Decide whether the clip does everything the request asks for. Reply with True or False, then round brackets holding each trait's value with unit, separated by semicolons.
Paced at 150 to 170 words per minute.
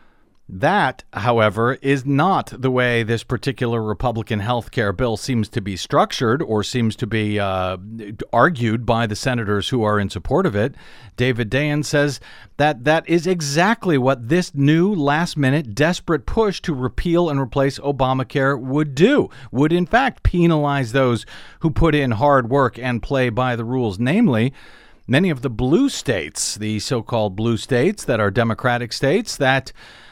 True (165 wpm)